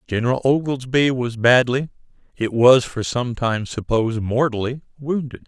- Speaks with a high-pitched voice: No, low, 125 Hz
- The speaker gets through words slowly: Yes, slow, 130 wpm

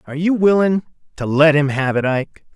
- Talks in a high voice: No, medium, 155 Hz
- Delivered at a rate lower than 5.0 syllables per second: No, 5.1 syllables/s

